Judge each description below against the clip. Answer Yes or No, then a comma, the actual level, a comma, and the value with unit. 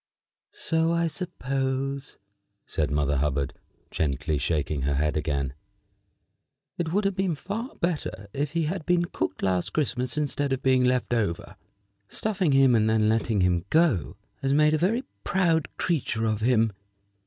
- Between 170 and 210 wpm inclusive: No, average, 155 wpm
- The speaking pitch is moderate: No, low, 130 Hz